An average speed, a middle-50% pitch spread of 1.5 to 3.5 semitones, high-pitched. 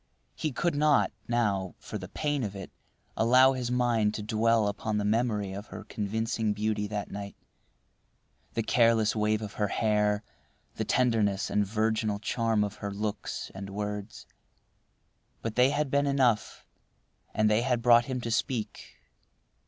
No: average, 150 wpm; narrow, 2.5 semitones; low, 110 Hz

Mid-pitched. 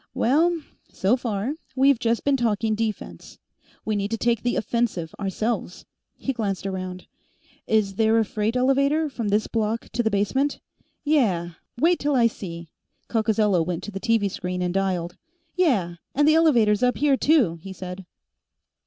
No: high, 220 Hz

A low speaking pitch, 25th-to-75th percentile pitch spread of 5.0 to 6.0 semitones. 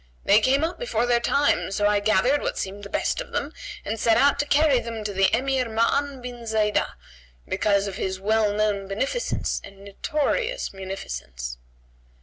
No: high, 220 Hz; wide, 5.4 semitones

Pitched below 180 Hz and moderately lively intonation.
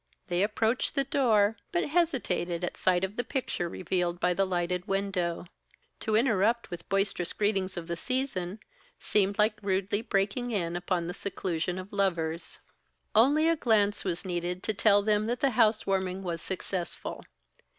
No: high, 195 Hz; average, 3.5 semitones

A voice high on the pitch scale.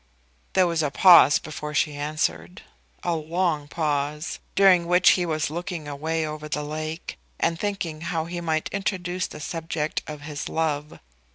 No: medium, 160 Hz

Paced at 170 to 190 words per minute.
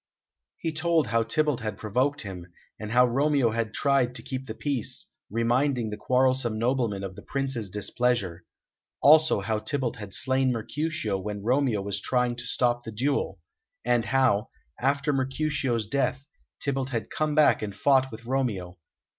No: average, 160 wpm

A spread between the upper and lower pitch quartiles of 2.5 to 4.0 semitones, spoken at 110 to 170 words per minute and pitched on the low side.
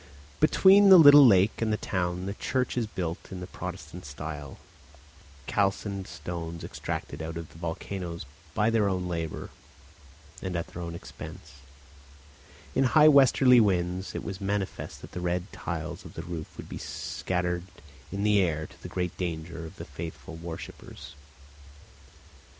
Yes: average, 3.5 semitones; average, 160 wpm; very low, 90 Hz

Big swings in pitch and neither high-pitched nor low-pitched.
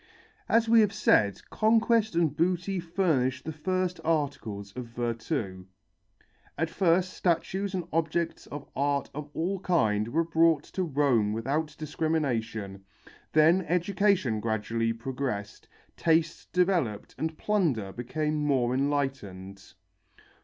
Yes: wide, 7.0 semitones; medium, 150 Hz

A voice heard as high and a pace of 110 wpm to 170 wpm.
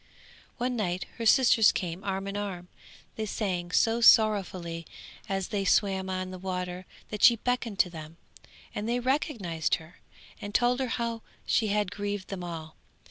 Yes: high, 200 Hz; average, 165 wpm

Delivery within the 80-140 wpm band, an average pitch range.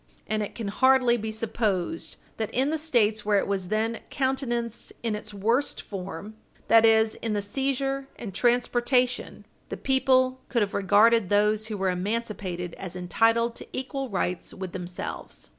No: average, 160 wpm; average, 3.6 semitones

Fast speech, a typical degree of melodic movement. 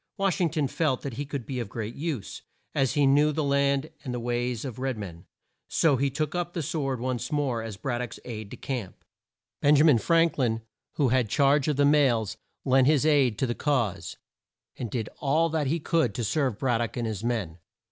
Yes: fast, 220 wpm; average, 3.9 semitones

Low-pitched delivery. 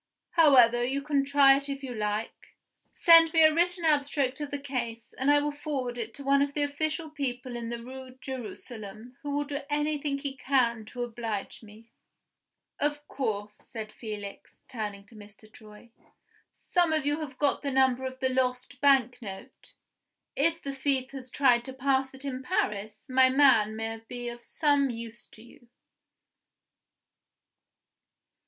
No: very high, 260 Hz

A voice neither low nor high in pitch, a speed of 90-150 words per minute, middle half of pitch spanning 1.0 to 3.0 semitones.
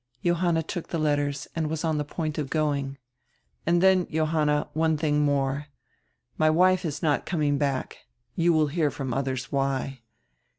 No: medium, 150 Hz; average, 165 wpm; narrow, 2.5 semitones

